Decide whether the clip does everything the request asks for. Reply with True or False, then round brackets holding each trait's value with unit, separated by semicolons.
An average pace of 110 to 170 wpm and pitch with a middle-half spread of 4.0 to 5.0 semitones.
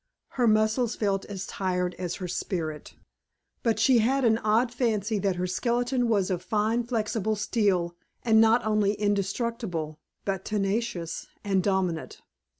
False (145 wpm; 3.6 semitones)